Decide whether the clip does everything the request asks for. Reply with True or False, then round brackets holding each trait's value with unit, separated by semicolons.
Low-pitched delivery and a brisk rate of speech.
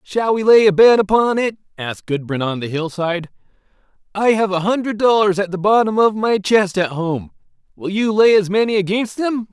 False (200 Hz; 210 wpm)